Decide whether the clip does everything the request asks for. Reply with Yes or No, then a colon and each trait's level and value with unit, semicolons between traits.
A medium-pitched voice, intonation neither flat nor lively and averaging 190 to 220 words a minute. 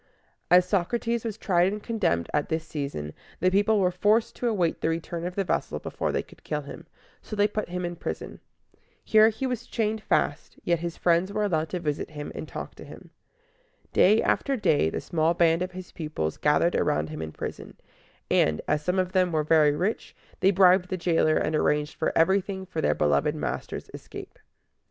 Yes: medium, 180 Hz; average, 4.3 semitones; average, 200 wpm